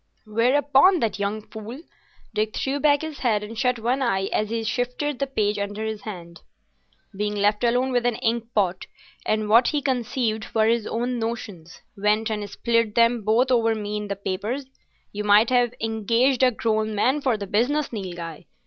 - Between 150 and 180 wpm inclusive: Yes, average, 175 wpm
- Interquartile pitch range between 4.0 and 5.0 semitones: No, average, 2.9 semitones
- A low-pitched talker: No, high, 225 Hz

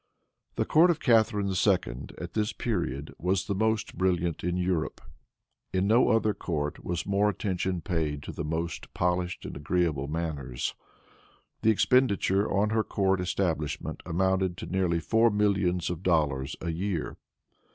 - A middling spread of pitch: Yes, average, 3.7 semitones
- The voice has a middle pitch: No, very low, 90 Hz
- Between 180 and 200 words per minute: No, average, 150 wpm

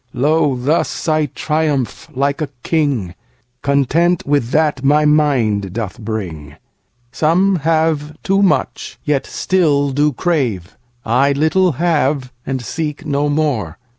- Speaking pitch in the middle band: Yes, medium, 145 Hz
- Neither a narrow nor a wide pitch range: Yes, average, 4.3 semitones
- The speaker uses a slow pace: Yes, slow, 110 wpm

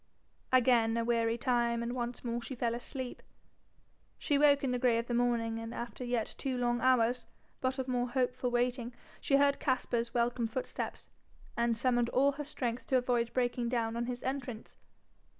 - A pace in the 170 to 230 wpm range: Yes, average, 180 wpm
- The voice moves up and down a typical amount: No, narrow, 1.5 semitones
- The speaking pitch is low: No, high, 245 Hz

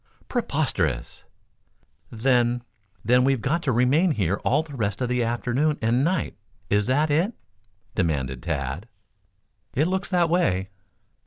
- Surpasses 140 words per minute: No, slow, 135 wpm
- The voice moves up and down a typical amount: No, wide, 7.1 semitones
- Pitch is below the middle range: Yes, low, 125 Hz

